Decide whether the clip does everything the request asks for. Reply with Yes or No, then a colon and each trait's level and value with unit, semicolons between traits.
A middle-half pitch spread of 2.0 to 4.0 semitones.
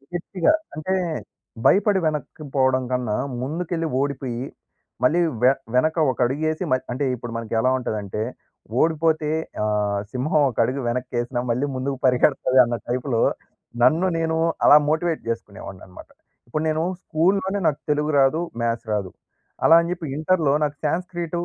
No: average, 4.7 semitones